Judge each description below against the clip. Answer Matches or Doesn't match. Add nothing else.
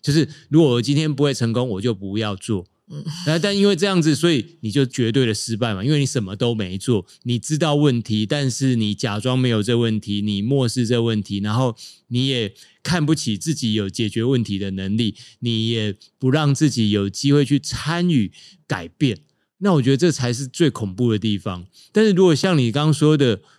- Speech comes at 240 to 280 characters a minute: Doesn't match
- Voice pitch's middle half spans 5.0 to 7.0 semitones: Matches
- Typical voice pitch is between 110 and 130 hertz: Matches